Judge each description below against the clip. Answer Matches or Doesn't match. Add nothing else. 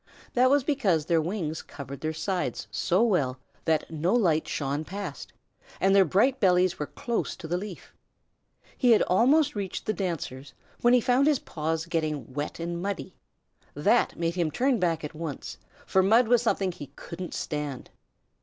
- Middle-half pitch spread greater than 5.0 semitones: Matches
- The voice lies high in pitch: Doesn't match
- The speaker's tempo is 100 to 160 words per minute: Doesn't match